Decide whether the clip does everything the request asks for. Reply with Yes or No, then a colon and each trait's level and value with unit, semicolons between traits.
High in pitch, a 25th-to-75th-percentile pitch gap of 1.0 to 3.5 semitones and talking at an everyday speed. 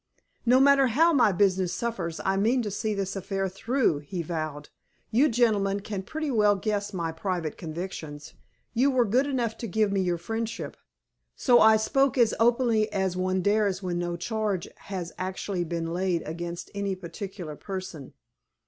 No: high, 195 Hz; average, 4.3 semitones; average, 165 wpm